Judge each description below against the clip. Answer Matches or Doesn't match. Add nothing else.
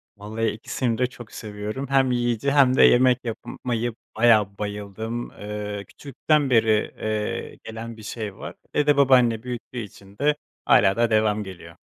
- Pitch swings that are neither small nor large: Matches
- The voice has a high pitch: Doesn't match